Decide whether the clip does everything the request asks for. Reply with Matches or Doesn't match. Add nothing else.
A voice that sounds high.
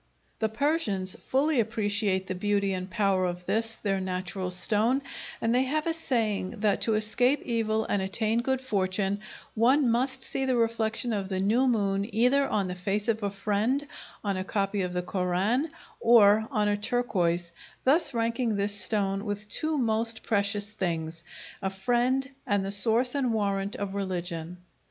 Matches